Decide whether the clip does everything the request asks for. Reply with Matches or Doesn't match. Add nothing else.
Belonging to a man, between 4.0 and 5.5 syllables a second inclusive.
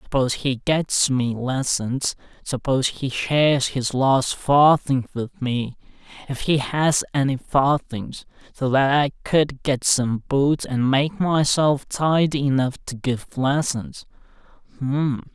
Doesn't match